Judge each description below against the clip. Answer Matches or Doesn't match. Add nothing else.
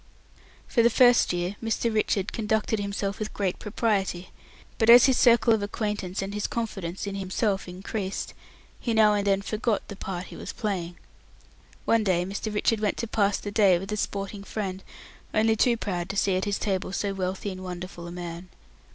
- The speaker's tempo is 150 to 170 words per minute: Doesn't match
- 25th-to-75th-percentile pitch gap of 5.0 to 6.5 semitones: Doesn't match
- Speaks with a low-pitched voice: Doesn't match